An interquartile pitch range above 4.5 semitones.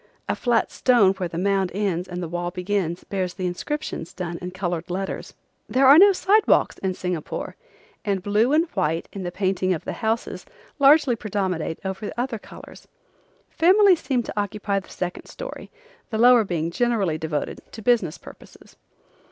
Yes: average, 5.2 semitones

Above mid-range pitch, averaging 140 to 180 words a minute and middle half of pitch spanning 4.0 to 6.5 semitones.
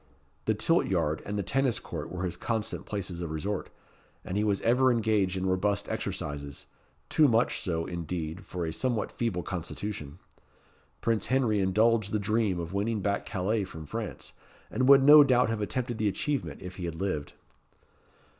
No: low, 100 Hz; average, 175 wpm; average, 4.3 semitones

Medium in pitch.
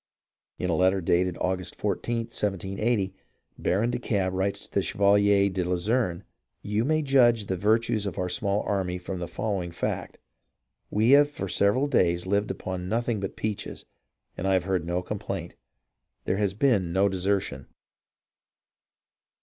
No: low, 100 Hz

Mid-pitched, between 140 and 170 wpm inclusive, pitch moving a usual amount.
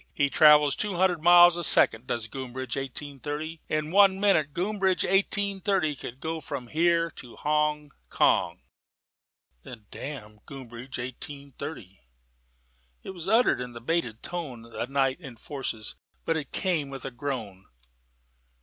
Yes: medium, 145 Hz; average, 145 wpm; average, 5.0 semitones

